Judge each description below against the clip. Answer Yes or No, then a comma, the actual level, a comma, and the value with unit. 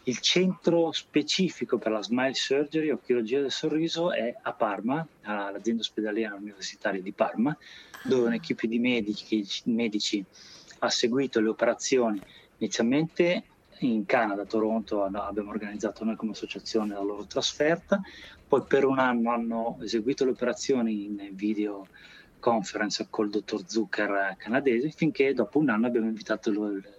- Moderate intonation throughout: Yes, average, 4.4 semitones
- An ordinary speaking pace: Yes, average, 140 wpm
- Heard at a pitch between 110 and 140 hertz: Yes, low, 115 Hz